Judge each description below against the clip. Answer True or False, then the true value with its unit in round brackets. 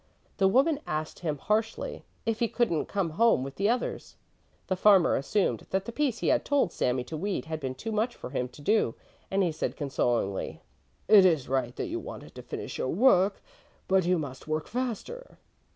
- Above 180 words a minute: True (200 wpm)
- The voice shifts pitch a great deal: True (7.1 semitones)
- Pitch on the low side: False (185 Hz)